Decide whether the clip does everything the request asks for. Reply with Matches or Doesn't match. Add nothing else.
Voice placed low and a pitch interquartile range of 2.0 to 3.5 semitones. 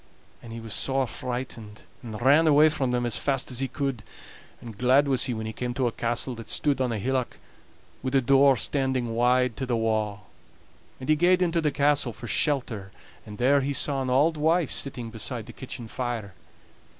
Matches